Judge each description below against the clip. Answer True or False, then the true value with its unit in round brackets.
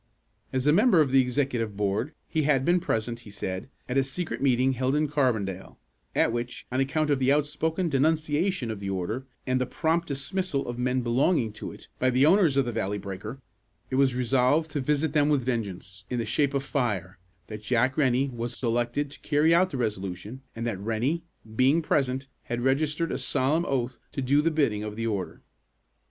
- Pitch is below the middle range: True (130 Hz)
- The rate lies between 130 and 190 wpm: False (200 wpm)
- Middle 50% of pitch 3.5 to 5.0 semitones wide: True (4.2 semitones)